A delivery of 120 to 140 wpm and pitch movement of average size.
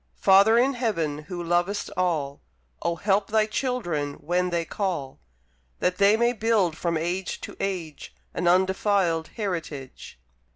Yes: slow, 135 wpm; average, 3.8 semitones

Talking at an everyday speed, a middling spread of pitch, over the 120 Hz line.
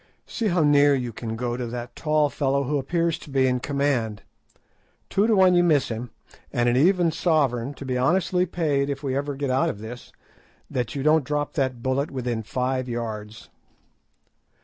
Yes: average, 190 wpm; average, 3.6 semitones; low, 135 Hz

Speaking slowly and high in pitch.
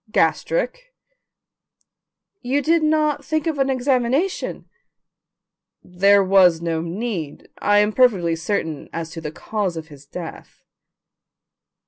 Yes: slow, 115 wpm; high, 205 Hz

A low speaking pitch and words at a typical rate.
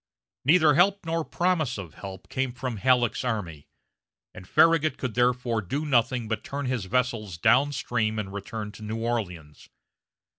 Yes: low, 120 Hz; average, 155 wpm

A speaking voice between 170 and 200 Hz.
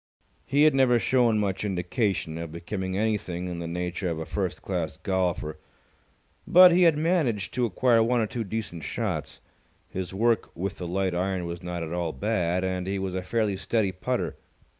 No: very low, 95 Hz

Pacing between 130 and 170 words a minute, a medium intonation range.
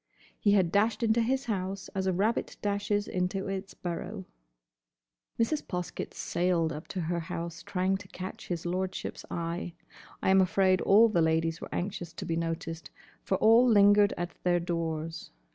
Yes: average, 165 wpm; average, 3.1 semitones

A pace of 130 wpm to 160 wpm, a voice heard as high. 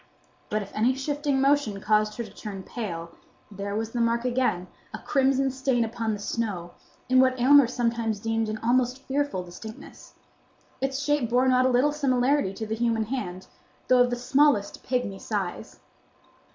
No: average, 170 wpm; high, 240 Hz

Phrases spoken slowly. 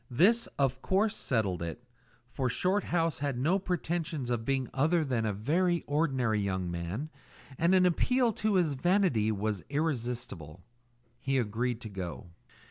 No: average, 145 wpm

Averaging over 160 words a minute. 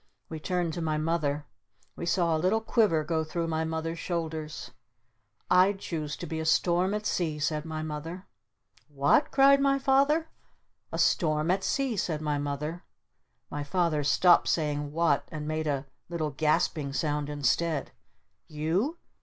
No: average, 155 wpm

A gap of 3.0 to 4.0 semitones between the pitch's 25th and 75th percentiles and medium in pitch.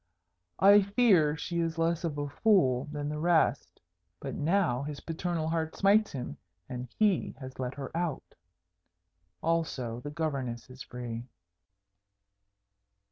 No: average, 4.7 semitones; medium, 155 Hz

